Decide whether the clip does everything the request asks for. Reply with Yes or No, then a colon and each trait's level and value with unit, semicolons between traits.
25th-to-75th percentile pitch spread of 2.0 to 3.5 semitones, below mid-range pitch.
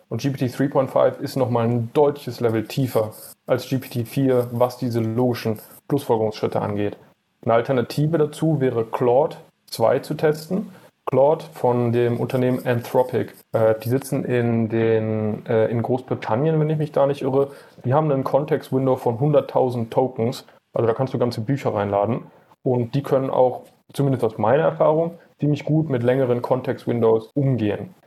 Yes: average, 3.1 semitones; low, 125 Hz